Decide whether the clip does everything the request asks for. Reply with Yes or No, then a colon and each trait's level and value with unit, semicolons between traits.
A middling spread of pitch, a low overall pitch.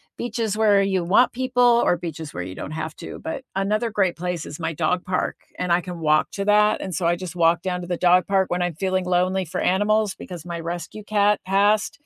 No: average, 3.2 semitones; medium, 185 Hz